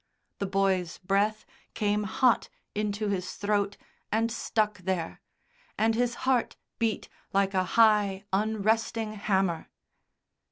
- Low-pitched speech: No, high, 205 Hz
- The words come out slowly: Yes, slow, 115 wpm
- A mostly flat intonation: Yes, narrow, 2.2 semitones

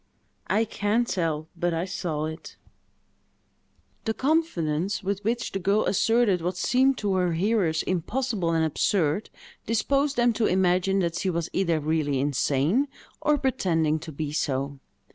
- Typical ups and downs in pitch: No, wide, 5.7 semitones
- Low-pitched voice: No, medium, 185 Hz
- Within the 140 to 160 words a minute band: Yes, average, 145 wpm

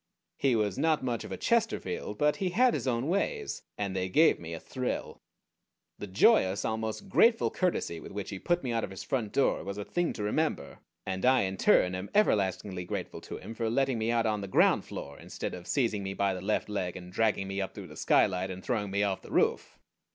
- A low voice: Yes, low, 105 Hz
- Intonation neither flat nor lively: No, wide, 5.7 semitones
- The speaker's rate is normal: No, fast, 230 wpm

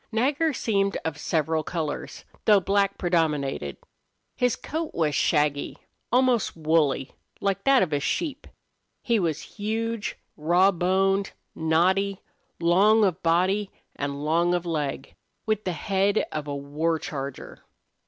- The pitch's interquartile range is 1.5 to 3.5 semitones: No, average, 4.8 semitones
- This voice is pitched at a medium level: Yes, medium, 175 Hz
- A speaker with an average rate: No, slow, 130 wpm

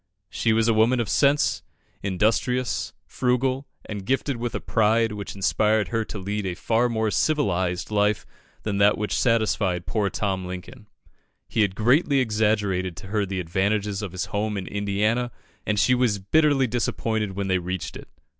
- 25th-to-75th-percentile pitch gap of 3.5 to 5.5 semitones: No, average, 2.9 semitones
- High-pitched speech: No, low, 105 Hz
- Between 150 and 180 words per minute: Yes, average, 170 wpm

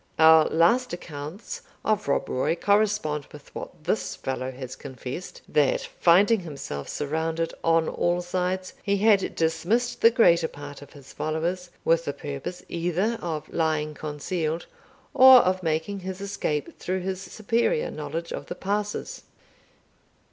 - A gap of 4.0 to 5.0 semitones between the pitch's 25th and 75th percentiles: Yes, average, 4.3 semitones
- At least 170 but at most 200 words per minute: No, average, 140 wpm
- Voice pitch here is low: No, medium, 170 Hz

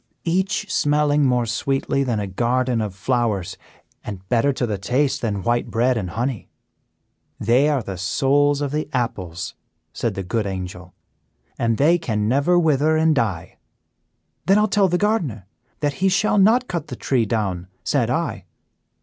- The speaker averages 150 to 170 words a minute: Yes, average, 160 wpm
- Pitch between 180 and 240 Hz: No, low, 125 Hz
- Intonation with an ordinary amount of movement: No, wide, 6.1 semitones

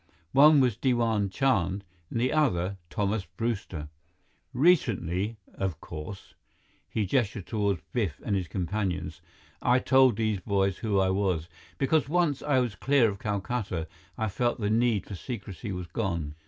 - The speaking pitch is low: Yes, low, 105 Hz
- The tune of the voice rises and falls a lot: No, average, 4.5 semitones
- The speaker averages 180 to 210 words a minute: No, average, 145 wpm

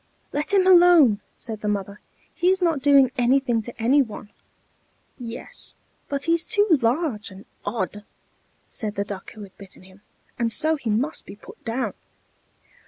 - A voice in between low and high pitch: No, high, 240 Hz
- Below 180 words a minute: Yes, average, 165 wpm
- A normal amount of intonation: No, wide, 6.7 semitones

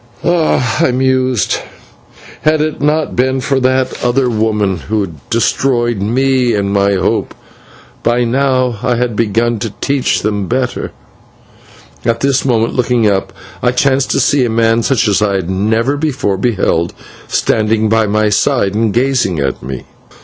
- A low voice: Yes, low, 120 Hz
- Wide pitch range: No, average, 3.7 semitones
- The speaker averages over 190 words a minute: No, average, 155 wpm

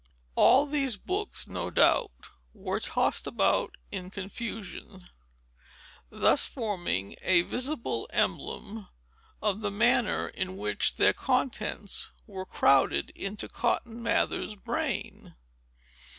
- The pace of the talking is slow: Yes, slow, 105 wpm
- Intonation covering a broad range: No, average, 4.1 semitones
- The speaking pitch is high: Yes, high, 210 Hz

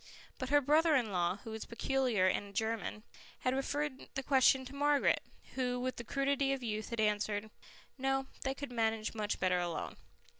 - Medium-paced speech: Yes, average, 185 wpm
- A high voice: Yes, very high, 250 Hz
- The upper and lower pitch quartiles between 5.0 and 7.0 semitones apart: No, average, 4.0 semitones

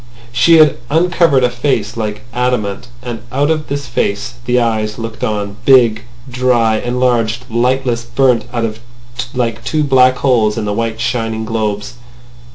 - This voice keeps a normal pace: Yes, average, 150 wpm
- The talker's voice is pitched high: No, low, 120 Hz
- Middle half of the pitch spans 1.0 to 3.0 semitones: Yes, narrow, 2.6 semitones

